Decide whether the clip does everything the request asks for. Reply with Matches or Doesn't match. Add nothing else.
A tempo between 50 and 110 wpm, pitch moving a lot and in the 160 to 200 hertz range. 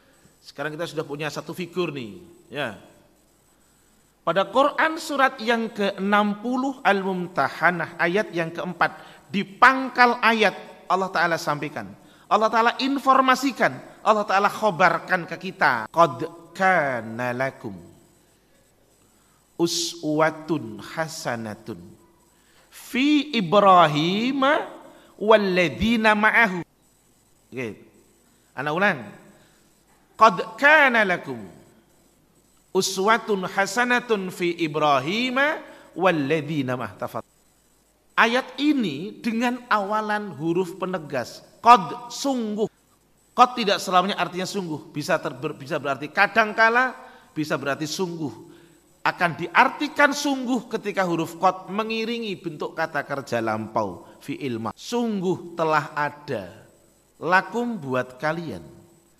Matches